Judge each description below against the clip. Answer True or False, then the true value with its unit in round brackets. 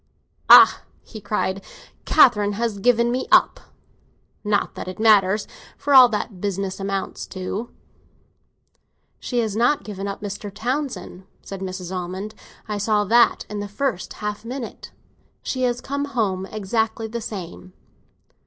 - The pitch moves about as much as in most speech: True (3.3 semitones)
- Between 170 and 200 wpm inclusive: False (145 wpm)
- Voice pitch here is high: True (210 Hz)